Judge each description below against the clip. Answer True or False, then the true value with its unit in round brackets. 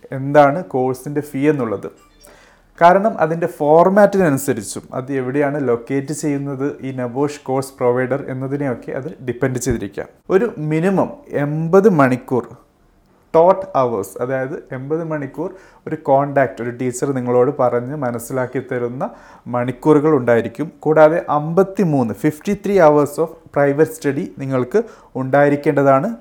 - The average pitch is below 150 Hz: True (140 Hz)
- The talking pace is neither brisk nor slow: True (110 wpm)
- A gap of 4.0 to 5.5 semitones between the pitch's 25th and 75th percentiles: False (3.4 semitones)